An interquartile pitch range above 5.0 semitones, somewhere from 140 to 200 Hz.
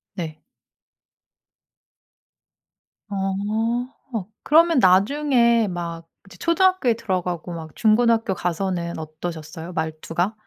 Yes: wide, 5.5 semitones; high, 190 Hz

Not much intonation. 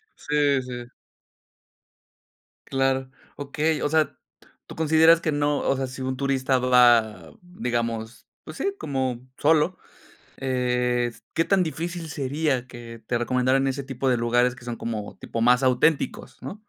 No: average, 3.2 semitones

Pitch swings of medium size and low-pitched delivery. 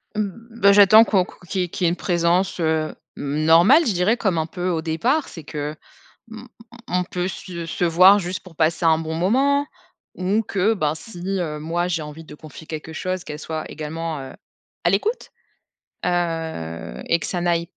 No: average, 3.4 semitones; medium, 175 Hz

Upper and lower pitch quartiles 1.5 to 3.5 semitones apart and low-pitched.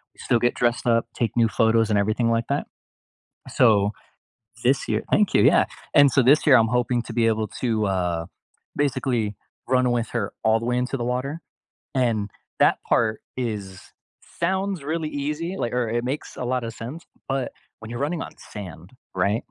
Yes: average, 3.1 semitones; low, 120 Hz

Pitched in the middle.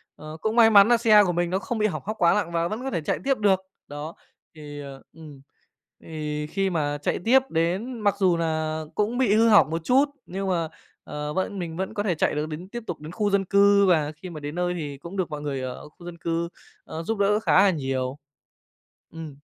Yes: medium, 175 Hz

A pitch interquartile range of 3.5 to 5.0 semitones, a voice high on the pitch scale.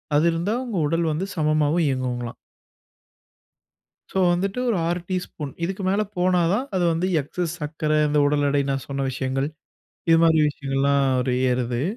No: average, 4.3 semitones; medium, 155 Hz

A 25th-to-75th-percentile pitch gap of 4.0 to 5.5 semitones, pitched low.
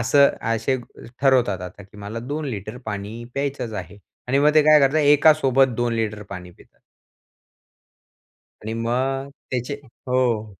Yes: average, 4.4 semitones; low, 120 Hz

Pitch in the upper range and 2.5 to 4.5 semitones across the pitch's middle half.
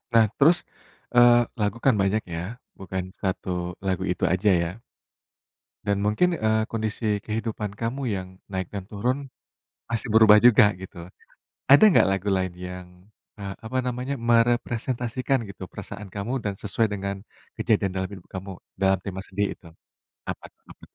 No: low, 105 Hz; average, 3.5 semitones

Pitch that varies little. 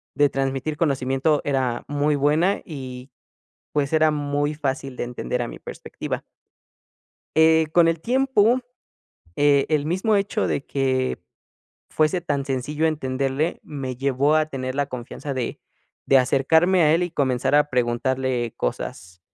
No: average, 3.2 semitones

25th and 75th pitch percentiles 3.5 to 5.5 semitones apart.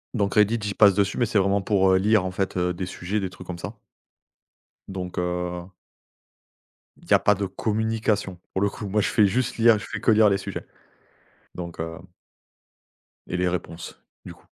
No: average, 2.8 semitones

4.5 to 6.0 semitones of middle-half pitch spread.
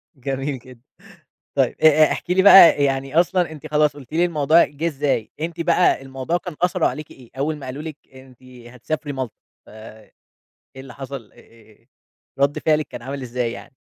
No: average, 3.4 semitones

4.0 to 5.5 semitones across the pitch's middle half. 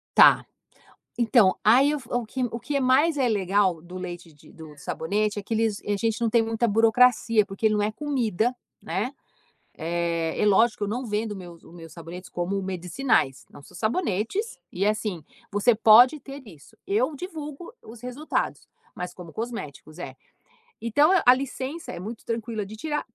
Yes: average, 5.2 semitones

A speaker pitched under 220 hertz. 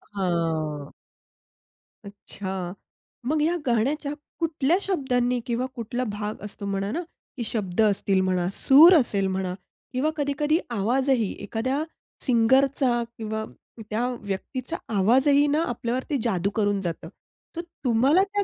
No: high, 235 Hz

